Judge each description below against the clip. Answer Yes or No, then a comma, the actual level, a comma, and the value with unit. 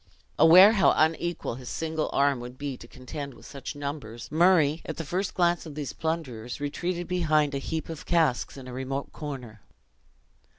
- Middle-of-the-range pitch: Yes, medium, 150 Hz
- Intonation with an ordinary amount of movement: Yes, average, 3.7 semitones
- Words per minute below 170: No, average, 175 wpm